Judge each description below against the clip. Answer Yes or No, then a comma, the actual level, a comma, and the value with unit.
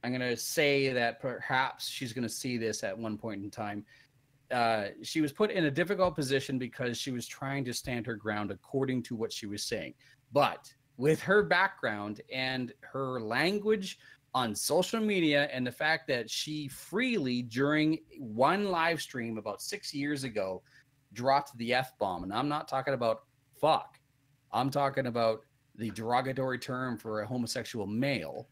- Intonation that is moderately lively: Yes, average, 3.7 semitones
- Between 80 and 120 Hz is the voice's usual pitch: No, low, 130 Hz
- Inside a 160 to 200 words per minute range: Yes, average, 175 wpm